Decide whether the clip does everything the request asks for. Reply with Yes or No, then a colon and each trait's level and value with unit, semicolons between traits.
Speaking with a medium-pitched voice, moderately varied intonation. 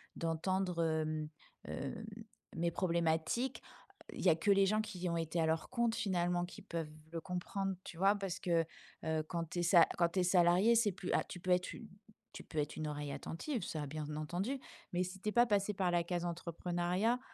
Yes: medium, 175 Hz; average, 3.0 semitones